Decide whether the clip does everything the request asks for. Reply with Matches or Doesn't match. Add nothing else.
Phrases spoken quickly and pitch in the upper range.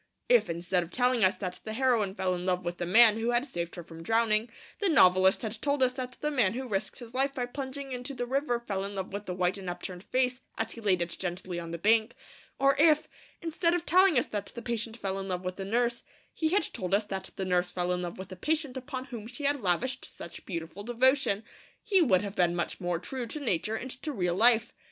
Matches